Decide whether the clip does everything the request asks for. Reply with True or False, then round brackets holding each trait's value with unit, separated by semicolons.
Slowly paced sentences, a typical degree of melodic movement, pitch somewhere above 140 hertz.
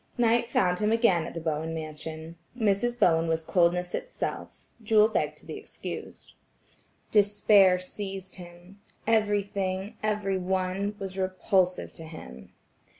True (130 wpm; 3.2 semitones; 190 Hz)